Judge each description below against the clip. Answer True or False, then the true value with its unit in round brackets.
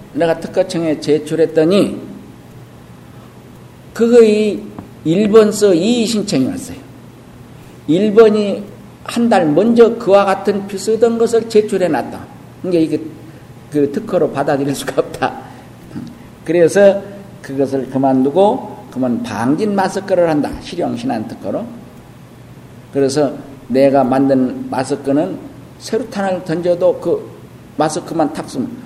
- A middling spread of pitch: False (7.1 semitones)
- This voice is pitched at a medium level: True (180 Hz)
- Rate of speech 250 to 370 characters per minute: False (235 characters per minute)